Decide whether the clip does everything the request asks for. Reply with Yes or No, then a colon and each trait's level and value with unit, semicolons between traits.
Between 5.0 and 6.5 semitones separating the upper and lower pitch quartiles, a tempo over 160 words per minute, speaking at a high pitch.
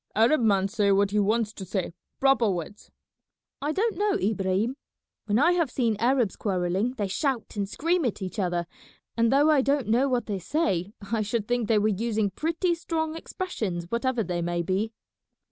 Yes: wide, 5.6 semitones; average, 185 wpm; high, 220 Hz